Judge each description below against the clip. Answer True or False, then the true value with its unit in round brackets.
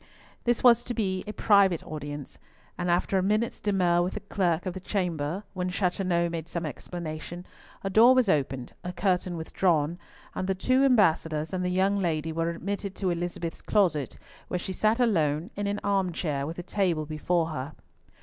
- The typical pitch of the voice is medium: True (180 Hz)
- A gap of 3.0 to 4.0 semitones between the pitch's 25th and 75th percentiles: True (3.5 semitones)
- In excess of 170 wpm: True (185 wpm)